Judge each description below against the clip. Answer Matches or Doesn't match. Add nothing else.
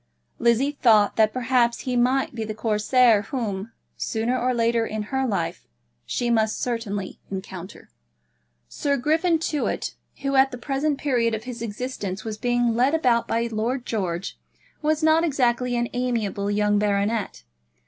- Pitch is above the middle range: Matches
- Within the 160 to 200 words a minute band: Doesn't match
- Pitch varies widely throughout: Doesn't match